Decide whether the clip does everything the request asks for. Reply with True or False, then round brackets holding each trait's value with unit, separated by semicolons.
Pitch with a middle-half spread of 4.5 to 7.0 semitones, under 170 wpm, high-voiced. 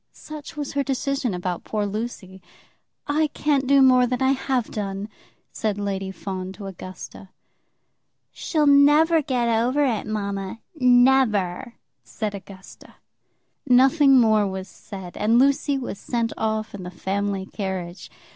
True (5.5 semitones; 135 wpm; 225 Hz)